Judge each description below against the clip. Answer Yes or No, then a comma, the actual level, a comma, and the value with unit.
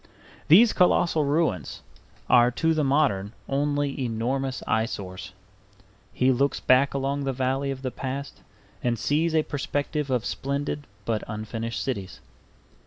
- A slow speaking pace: Yes, slow, 130 wpm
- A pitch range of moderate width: Yes, average, 3.3 semitones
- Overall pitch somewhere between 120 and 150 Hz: Yes, low, 135 Hz